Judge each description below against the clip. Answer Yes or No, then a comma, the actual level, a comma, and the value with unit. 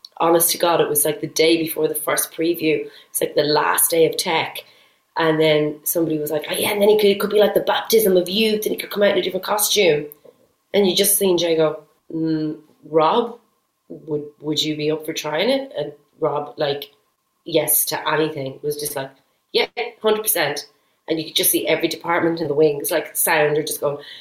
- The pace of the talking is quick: Yes, fast, 225 wpm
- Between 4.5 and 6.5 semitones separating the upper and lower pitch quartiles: Yes, average, 4.9 semitones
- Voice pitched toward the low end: No, medium, 160 Hz